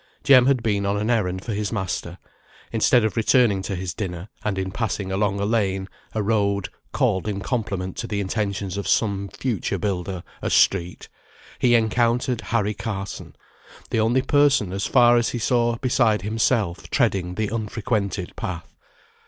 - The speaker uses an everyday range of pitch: Yes, average, 3.2 semitones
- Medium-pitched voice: No, low, 105 Hz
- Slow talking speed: No, average, 165 wpm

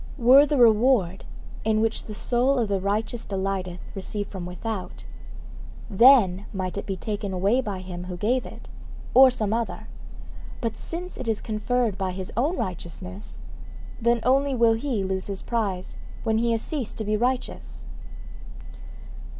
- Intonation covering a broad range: No, average, 4.1 semitones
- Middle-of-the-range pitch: No, high, 215 Hz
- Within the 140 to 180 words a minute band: Yes, average, 160 wpm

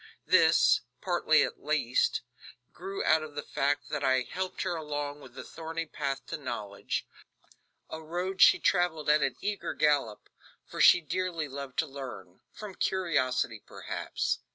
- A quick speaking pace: No, average, 150 wpm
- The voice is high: No, medium, 150 Hz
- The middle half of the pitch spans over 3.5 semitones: Yes, average, 4.4 semitones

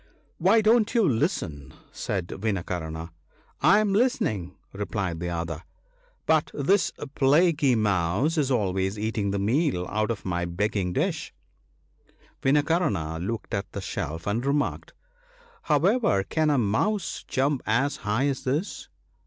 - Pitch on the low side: Yes, low, 115 Hz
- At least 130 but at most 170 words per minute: Yes, average, 150 wpm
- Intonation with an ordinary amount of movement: No, wide, 8.8 semitones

